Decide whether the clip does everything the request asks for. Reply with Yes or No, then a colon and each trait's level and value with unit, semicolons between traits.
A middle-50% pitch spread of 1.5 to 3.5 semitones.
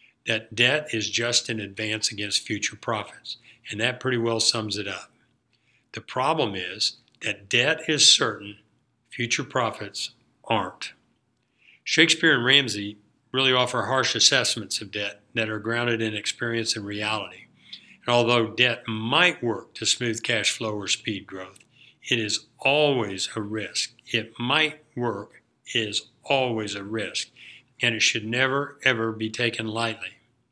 Yes: narrow, 2.4 semitones